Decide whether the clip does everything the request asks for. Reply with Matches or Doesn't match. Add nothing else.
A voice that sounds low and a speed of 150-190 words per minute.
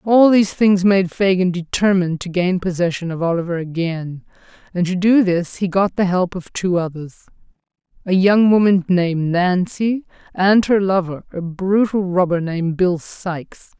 Doesn't match